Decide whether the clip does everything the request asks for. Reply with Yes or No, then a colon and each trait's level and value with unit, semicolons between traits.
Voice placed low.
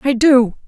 No: very high, 255 Hz